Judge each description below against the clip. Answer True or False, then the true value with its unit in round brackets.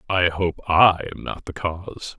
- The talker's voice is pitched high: False (90 Hz)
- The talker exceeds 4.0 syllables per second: True (4.2 syllables/s)